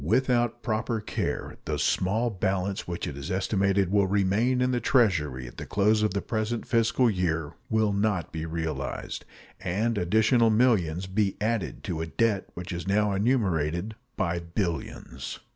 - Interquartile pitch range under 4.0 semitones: No, average, 4.3 semitones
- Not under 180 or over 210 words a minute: No, average, 160 wpm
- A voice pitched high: No, low, 100 Hz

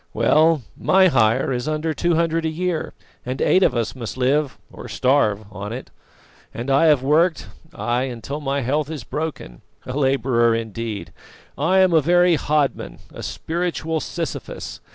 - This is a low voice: No, medium, 145 Hz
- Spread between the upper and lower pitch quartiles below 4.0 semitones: No, average, 4.8 semitones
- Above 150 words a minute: Yes, average, 160 wpm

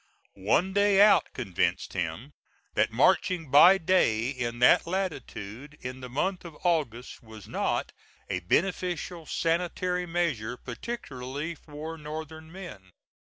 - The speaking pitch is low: No, medium, 160 Hz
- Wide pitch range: Yes, wide, 6.2 semitones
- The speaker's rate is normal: No, slow, 120 wpm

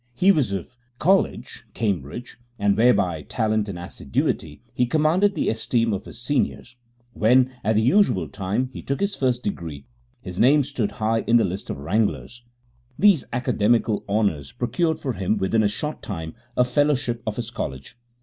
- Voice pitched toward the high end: No, low, 115 Hz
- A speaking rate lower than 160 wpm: No, average, 170 wpm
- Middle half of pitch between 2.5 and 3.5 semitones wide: No, average, 4.7 semitones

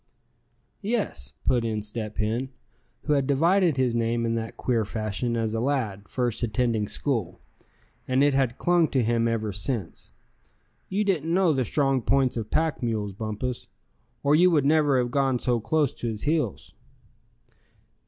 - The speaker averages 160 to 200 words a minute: Yes, average, 165 wpm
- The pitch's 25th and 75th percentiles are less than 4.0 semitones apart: No, average, 4.3 semitones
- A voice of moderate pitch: No, low, 125 Hz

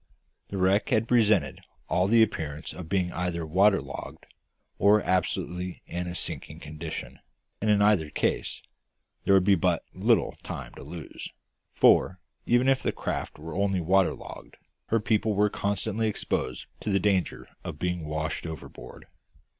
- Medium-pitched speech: No, very low, 95 Hz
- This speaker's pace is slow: No, average, 150 wpm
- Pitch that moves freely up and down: No, average, 3.9 semitones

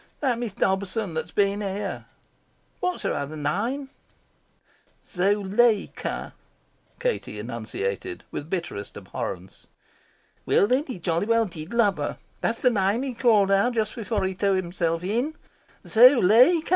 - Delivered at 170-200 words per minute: No, slow, 135 wpm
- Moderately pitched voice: No, high, 200 Hz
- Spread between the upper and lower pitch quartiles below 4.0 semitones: No, average, 5.3 semitones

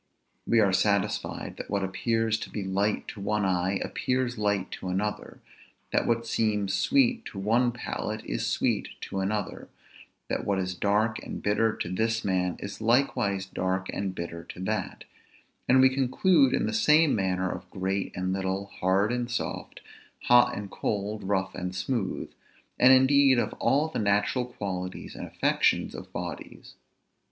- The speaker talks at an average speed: Yes, average, 165 wpm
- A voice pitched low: Yes, low, 105 Hz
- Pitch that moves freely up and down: No, average, 4.1 semitones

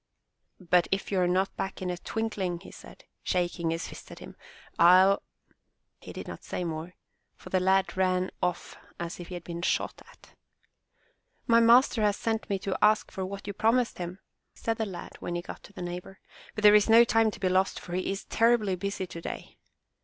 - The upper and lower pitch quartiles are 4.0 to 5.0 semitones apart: No, average, 2.9 semitones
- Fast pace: Yes, fast, 210 wpm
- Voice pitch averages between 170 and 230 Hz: Yes, high, 190 Hz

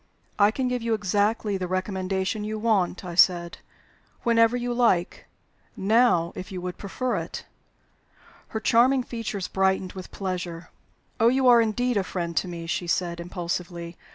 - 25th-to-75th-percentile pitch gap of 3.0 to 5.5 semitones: Yes, average, 4.3 semitones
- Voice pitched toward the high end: Yes, high, 195 Hz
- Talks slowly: No, average, 155 wpm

